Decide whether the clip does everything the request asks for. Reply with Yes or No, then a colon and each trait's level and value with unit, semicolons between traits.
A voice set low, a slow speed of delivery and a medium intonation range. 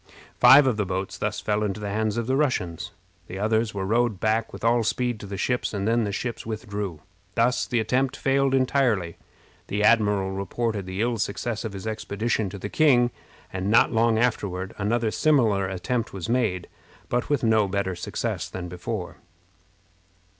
No: low, 110 Hz; average, 180 wpm; average, 3.3 semitones